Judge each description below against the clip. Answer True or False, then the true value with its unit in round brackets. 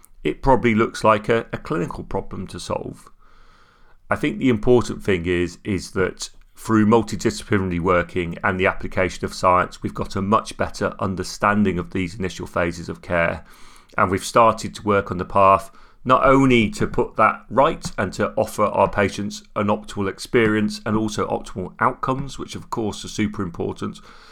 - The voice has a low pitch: True (100 Hz)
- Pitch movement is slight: False (3.1 semitones)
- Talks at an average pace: True (175 wpm)